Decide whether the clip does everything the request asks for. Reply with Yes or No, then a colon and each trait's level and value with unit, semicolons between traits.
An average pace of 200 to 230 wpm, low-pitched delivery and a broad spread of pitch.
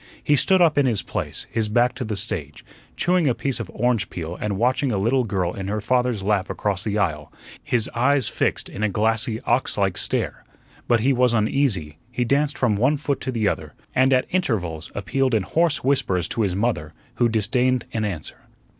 No: fast, 205 wpm; low, 115 Hz; average, 4.5 semitones